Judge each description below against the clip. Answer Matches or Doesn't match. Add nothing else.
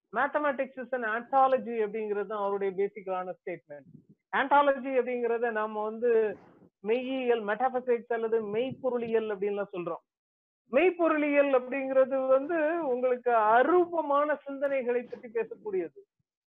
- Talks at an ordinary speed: Matches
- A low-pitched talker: Doesn't match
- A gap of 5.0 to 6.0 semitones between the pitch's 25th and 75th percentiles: Doesn't match